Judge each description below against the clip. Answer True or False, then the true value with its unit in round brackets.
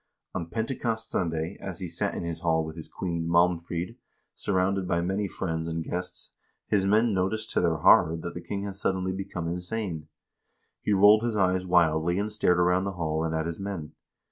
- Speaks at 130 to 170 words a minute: False (195 wpm)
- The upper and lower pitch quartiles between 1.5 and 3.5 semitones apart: True (2.9 semitones)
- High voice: False (90 Hz)